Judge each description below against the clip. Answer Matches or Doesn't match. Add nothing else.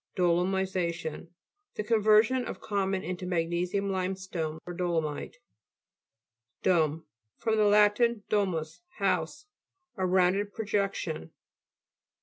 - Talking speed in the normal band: Doesn't match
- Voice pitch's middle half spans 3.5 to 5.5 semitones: Doesn't match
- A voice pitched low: Doesn't match